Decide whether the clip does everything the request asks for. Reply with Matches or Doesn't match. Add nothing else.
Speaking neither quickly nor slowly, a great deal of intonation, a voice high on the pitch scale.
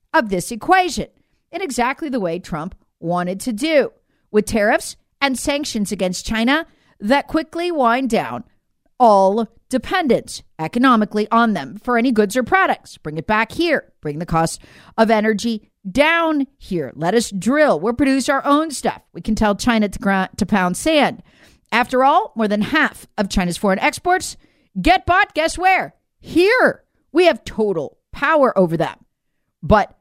Matches